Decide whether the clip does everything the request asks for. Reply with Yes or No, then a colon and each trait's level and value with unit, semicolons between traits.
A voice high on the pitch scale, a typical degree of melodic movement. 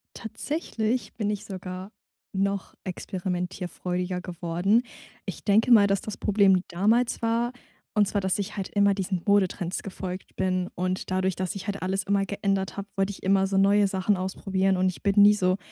No: high, 195 Hz; narrow, 1.6 semitones